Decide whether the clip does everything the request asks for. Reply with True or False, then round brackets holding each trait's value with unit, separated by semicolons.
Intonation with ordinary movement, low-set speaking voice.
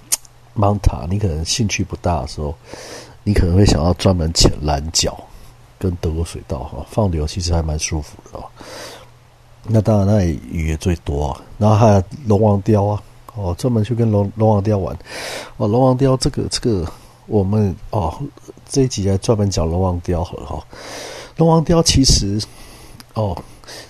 True (4.9 semitones; 100 Hz)